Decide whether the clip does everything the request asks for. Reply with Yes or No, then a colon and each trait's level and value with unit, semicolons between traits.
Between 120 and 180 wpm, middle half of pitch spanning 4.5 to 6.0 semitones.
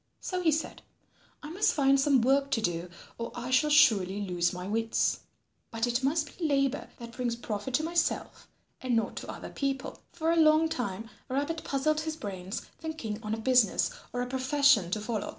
No: average, 190 wpm; average, 5.3 semitones